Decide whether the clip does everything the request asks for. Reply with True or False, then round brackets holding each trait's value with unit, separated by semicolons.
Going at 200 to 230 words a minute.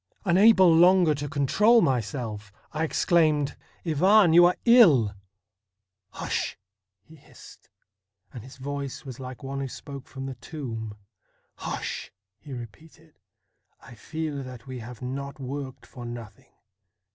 False (155 wpm)